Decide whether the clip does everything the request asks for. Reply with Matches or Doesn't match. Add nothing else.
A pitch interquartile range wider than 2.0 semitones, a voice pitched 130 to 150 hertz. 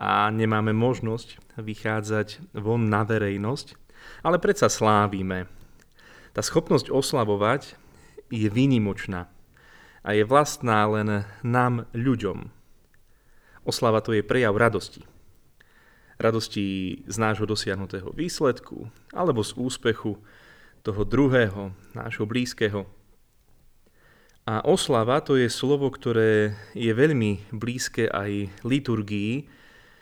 Doesn't match